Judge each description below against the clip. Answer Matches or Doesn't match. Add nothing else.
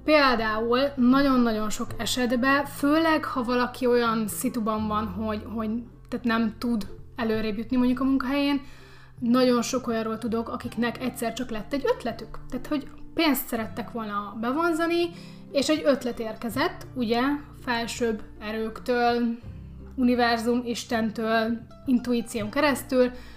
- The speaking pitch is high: Matches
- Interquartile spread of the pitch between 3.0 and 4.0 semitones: Doesn't match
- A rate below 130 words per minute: Matches